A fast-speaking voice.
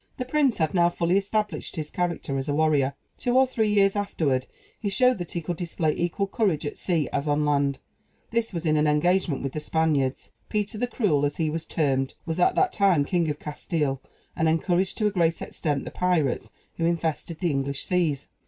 Yes: fast, 210 wpm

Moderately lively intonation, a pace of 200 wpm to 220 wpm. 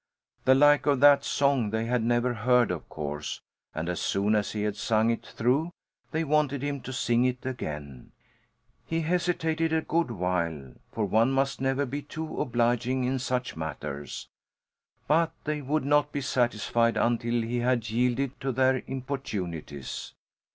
No: average, 4.4 semitones; average, 160 wpm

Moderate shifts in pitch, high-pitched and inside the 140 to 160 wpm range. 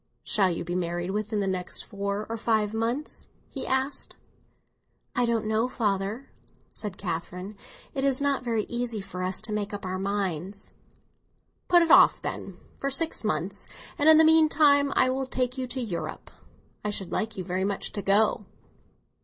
No: average, 5.0 semitones; high, 215 Hz; average, 175 wpm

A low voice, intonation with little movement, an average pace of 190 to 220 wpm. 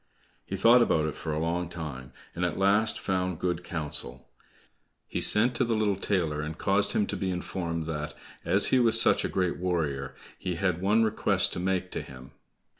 No: very low, 90 Hz; average, 4.0 semitones; average, 195 wpm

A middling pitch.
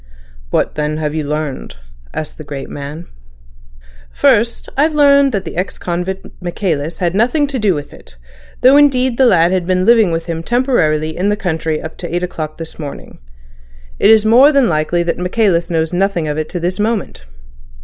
Yes: medium, 175 Hz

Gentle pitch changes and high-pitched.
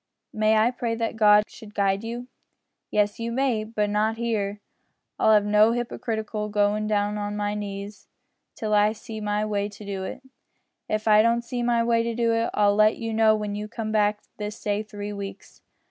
Yes: narrow, 1.6 semitones; high, 215 Hz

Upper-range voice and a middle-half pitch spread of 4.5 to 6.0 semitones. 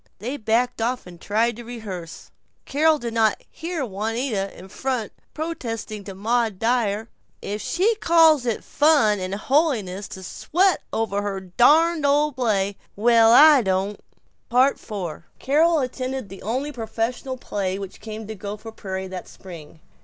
Yes: high, 225 Hz; average, 5.0 semitones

